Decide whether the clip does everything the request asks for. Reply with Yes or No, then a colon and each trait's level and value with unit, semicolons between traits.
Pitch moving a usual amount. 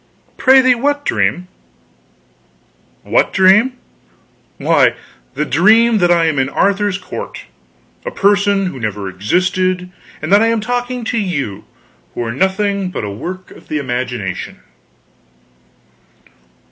No: wide, 7.3 semitones